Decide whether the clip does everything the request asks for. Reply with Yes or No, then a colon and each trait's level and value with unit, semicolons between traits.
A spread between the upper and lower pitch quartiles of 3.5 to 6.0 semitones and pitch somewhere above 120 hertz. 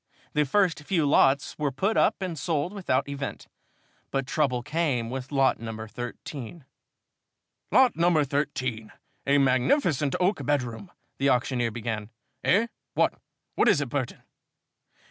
Yes: average, 4.6 semitones; medium, 140 Hz